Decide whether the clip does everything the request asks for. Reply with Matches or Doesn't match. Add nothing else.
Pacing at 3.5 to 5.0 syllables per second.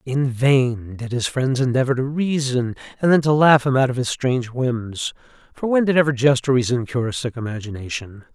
Doesn't match